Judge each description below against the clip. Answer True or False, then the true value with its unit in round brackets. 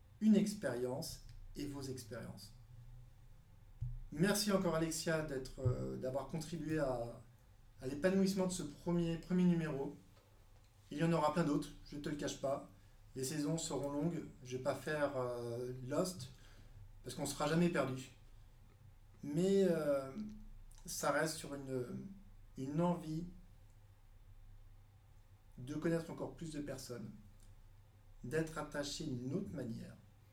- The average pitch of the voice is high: False (130 Hz)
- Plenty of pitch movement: True (6.5 semitones)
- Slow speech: True (130 wpm)